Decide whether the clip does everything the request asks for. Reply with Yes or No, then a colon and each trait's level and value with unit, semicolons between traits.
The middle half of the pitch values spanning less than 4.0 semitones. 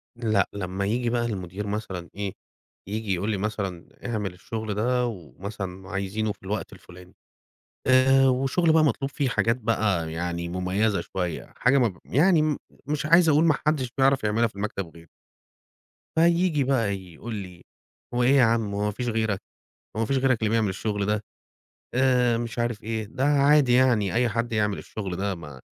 No: average, 4.5 semitones